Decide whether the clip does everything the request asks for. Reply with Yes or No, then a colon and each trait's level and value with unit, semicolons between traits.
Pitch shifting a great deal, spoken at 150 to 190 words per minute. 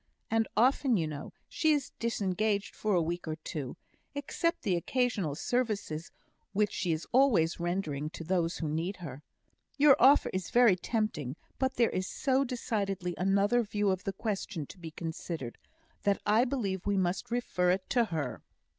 Yes: wide, 5.7 semitones; average, 170 wpm